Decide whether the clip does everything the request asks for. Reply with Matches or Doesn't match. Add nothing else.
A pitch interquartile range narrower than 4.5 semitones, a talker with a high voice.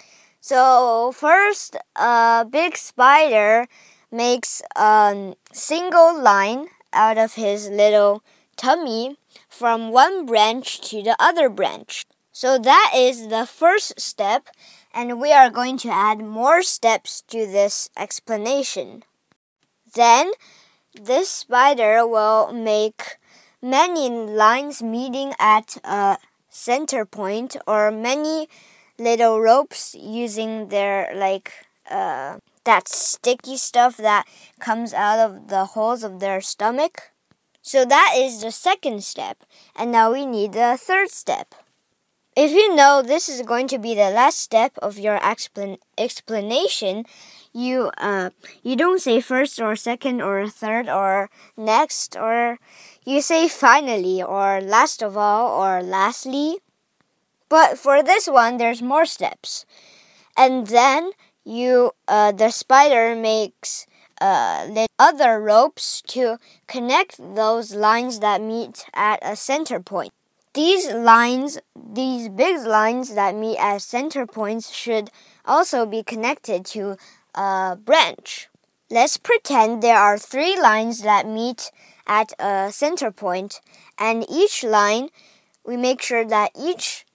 Matches